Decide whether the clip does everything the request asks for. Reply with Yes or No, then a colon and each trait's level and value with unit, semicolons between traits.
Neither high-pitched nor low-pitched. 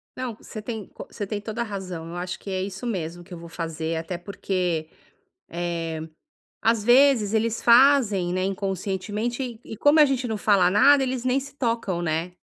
No: high, 200 Hz